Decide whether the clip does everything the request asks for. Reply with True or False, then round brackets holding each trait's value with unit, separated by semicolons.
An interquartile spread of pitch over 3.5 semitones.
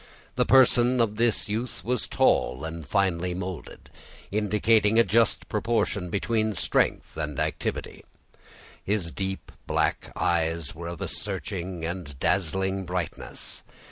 True (4.2 semitones)